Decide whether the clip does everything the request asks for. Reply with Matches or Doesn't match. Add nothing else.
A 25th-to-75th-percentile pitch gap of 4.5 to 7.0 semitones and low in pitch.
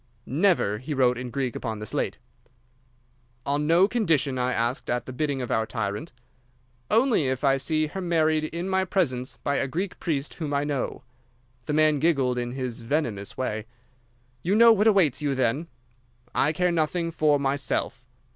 Doesn't match